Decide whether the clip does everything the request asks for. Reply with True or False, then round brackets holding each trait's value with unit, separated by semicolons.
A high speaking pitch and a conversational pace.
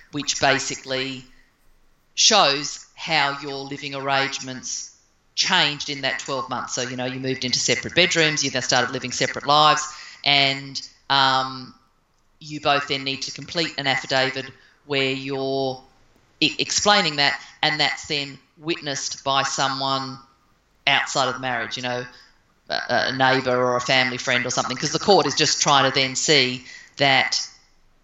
False (135 Hz; 155 wpm)